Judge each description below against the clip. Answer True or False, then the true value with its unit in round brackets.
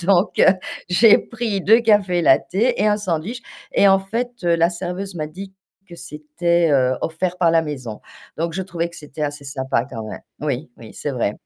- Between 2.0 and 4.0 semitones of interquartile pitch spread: False (4.5 semitones)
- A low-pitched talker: False (170 Hz)